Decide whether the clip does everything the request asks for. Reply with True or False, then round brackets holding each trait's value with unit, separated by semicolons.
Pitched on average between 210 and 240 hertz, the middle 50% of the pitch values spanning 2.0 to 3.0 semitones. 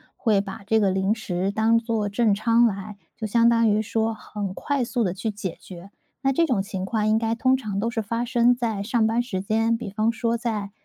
True (220 Hz; 2.4 semitones)